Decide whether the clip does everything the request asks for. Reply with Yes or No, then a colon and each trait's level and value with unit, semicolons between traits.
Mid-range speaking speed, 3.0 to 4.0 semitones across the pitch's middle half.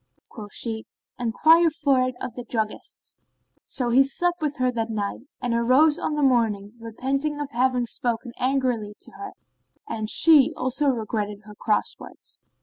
Yes: average, 160 wpm; average, 3.7 semitones